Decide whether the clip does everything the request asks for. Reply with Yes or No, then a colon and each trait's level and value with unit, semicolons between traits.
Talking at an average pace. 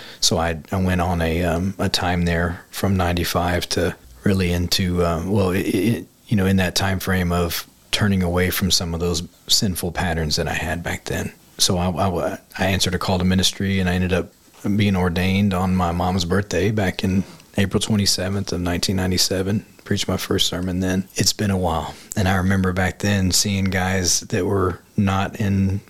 Yes: average, 195 wpm